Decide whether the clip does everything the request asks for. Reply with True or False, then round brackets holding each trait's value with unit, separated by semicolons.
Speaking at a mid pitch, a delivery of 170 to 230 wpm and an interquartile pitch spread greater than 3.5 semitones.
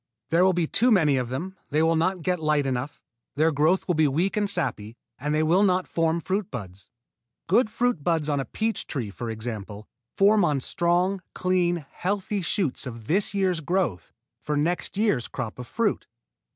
True (165 Hz; 190 wpm; 5.5 semitones)